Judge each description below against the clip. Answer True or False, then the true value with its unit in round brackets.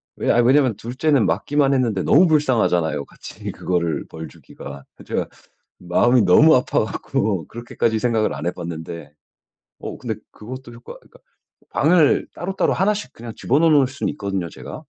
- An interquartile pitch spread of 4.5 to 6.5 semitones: False (7.7 semitones)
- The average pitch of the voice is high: False (120 Hz)